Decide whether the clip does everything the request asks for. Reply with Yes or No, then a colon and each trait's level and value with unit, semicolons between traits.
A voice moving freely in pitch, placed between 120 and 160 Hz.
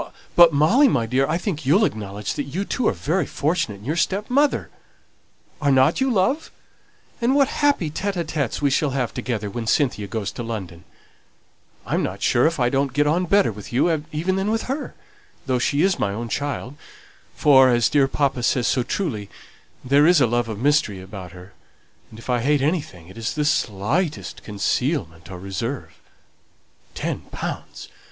Yes: wide, 6.7 semitones; medium, 140 Hz